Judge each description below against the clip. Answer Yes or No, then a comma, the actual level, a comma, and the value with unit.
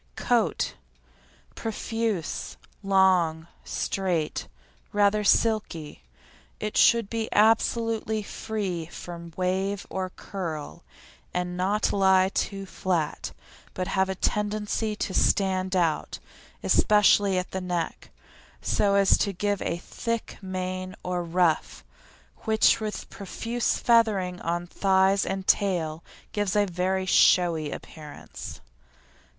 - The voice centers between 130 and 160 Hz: No, high, 190 Hz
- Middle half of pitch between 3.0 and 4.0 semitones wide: No, narrow, 2.6 semitones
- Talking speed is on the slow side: Yes, slow, 110 wpm